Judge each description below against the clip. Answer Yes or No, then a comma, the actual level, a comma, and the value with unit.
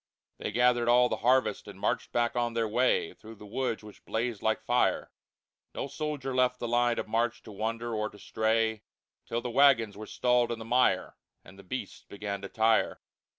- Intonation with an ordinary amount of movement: No, narrow, 2.0 semitones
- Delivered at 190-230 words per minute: Yes, average, 195 wpm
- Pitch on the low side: Yes, low, 115 Hz